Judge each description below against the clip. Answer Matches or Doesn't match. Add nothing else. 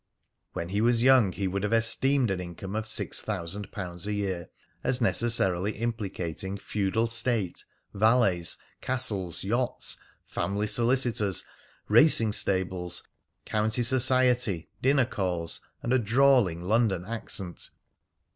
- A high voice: Doesn't match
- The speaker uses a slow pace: Matches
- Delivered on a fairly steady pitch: Doesn't match